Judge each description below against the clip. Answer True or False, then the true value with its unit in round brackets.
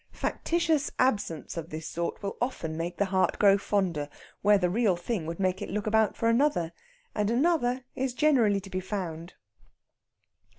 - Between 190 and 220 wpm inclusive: False (170 wpm)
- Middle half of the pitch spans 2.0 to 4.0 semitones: False (5.6 semitones)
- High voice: True (200 Hz)